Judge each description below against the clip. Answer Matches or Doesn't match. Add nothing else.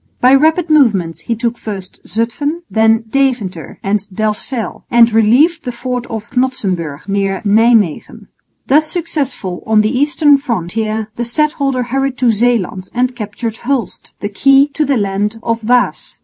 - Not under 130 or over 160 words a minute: Matches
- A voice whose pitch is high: Matches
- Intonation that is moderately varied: Matches